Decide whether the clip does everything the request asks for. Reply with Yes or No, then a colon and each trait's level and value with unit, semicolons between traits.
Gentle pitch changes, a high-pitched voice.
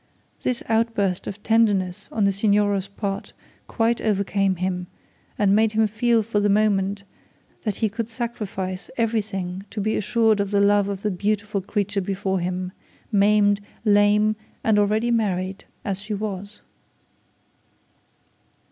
Yes: narrow, 1.8 semitones; high, 205 Hz